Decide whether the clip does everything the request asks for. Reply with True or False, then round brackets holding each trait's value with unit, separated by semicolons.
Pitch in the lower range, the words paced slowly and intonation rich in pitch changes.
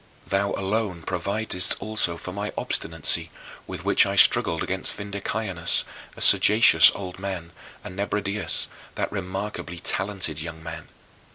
False (95 Hz; 125 wpm; 2.7 semitones)